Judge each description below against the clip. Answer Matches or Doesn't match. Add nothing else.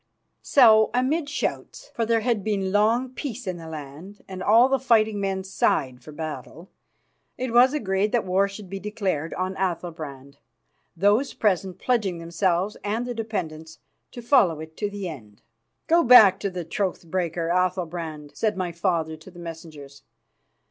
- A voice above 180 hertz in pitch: Matches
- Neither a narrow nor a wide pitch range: Matches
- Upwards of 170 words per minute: Doesn't match